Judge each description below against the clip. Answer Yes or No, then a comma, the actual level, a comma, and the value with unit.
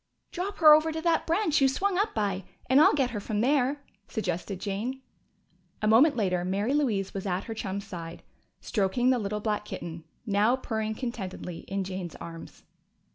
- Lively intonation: Yes, wide, 5.8 semitones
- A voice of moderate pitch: No, high, 220 Hz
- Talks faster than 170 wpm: Yes, average, 180 wpm